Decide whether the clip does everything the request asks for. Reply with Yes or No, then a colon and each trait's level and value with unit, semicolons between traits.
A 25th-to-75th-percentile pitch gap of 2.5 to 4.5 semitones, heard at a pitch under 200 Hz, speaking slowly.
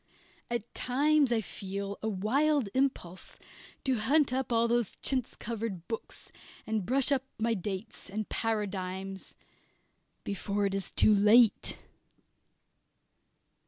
No: average, 4.0 semitones; high, 220 Hz; slow, 120 wpm